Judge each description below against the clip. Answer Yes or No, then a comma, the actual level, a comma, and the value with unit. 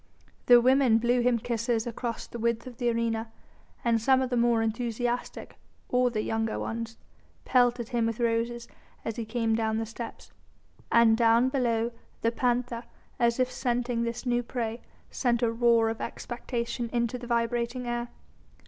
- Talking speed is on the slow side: No, average, 165 wpm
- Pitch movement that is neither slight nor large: No, narrow, 1.2 semitones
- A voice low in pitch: No, high, 235 Hz